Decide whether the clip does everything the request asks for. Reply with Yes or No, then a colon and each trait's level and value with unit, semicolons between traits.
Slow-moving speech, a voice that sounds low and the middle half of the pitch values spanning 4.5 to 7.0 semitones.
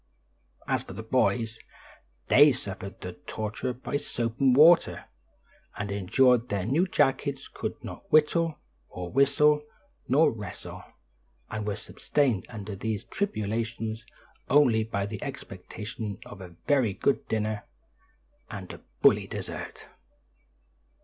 Yes: slow, 125 wpm; low, 115 Hz; average, 5.1 semitones